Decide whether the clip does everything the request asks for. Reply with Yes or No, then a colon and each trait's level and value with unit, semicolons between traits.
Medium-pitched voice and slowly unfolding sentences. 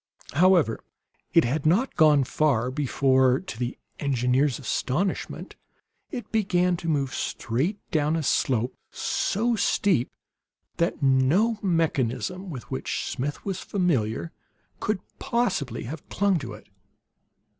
Yes: medium, 150 Hz; slow, 120 wpm